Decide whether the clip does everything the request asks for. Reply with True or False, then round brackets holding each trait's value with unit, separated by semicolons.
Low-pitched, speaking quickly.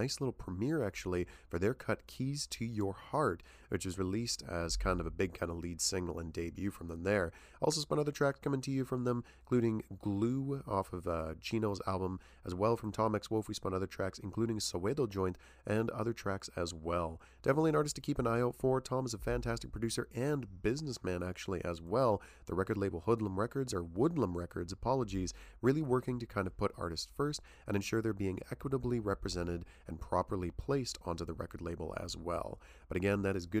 True (100 Hz; 210 wpm)